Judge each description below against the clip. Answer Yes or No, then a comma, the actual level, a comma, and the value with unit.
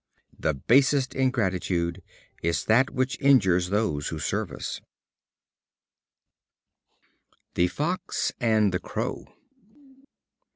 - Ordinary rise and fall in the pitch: No, wide, 6.9 semitones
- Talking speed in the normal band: No, slow, 90 wpm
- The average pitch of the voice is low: Yes, low, 105 Hz